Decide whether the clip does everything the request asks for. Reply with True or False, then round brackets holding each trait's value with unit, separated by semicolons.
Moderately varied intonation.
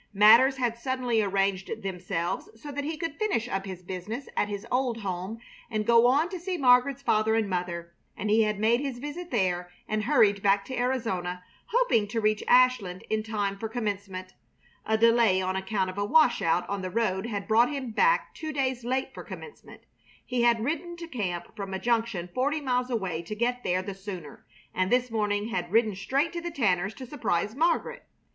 True (4.7 semitones)